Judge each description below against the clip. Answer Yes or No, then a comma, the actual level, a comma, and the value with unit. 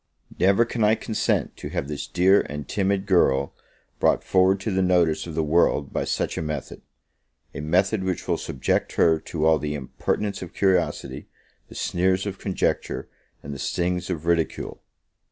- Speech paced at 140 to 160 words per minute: No, average, 170 wpm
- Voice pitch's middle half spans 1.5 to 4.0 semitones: Yes, average, 3.7 semitones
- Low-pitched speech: Yes, very low, 90 Hz